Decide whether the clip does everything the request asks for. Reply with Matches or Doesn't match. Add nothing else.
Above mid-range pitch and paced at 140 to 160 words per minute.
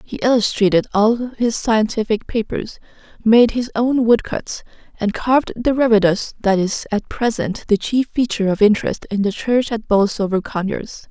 Matches